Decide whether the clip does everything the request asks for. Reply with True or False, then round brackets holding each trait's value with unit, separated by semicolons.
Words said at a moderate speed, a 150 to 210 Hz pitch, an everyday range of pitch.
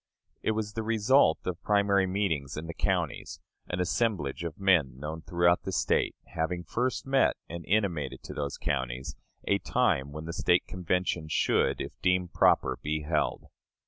False (165 wpm; 85 Hz; 4.5 semitones)